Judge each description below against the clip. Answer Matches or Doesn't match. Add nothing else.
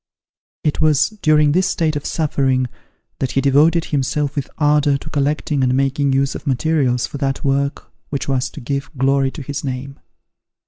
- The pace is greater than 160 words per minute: Matches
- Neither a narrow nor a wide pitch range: Doesn't match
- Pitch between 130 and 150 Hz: Matches